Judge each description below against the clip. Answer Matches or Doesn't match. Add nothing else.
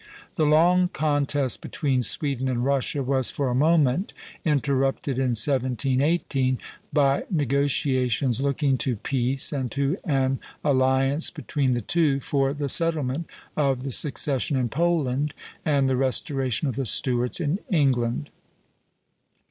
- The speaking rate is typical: Doesn't match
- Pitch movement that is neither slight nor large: Doesn't match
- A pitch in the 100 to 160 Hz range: Matches